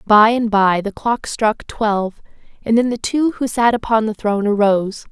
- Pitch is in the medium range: No, high, 220 Hz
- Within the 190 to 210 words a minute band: Yes, average, 200 wpm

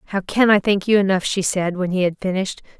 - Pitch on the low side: No, high, 190 Hz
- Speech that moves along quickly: Yes, fast, 260 wpm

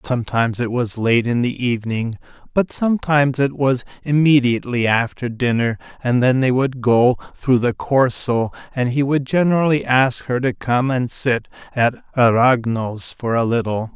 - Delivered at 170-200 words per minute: No, average, 160 wpm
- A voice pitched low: Yes, low, 125 Hz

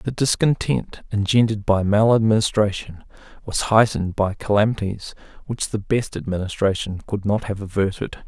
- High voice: No, low, 105 Hz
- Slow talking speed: Yes, slow, 125 wpm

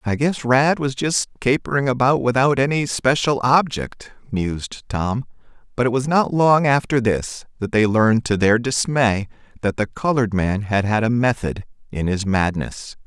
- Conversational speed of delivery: Yes, average, 170 wpm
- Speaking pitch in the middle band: No, low, 120 Hz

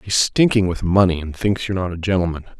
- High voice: No, very low, 90 Hz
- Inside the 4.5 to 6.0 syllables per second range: No, 6.3 syllables/s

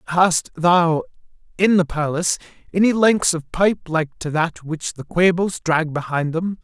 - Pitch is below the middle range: No, medium, 170 Hz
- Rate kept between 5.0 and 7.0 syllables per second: No, 4.3 syllables/s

